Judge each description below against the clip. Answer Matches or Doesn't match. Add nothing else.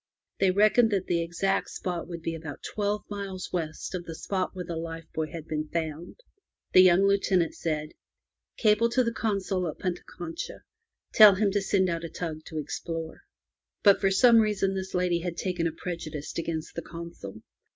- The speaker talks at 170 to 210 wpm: Matches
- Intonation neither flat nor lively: Matches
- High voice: Doesn't match